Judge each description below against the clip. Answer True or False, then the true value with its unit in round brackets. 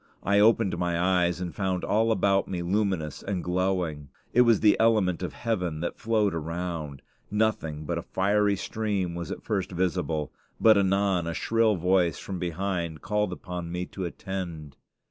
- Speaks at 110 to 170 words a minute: True (165 wpm)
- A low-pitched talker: True (90 Hz)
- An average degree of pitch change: True (3.0 semitones)